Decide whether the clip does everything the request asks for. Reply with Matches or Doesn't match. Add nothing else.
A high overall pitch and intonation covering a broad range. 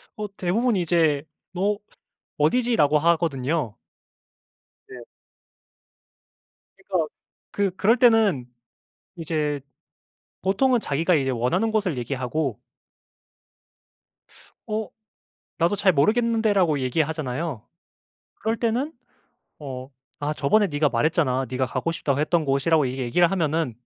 Doesn't match